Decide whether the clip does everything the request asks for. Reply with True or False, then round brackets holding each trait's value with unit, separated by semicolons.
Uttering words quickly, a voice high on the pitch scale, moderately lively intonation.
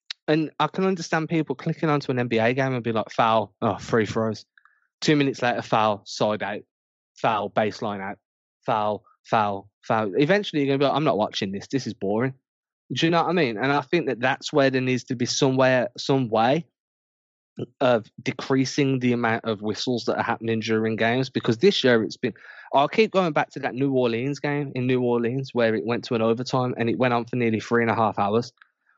False (220 wpm; 125 Hz; 3.7 semitones)